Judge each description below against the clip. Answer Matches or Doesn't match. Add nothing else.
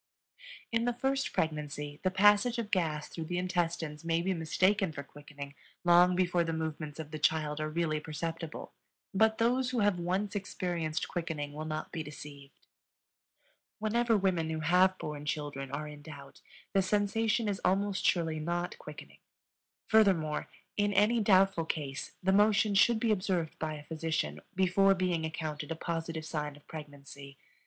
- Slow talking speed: Doesn't match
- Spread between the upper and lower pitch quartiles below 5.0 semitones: Matches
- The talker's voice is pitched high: Doesn't match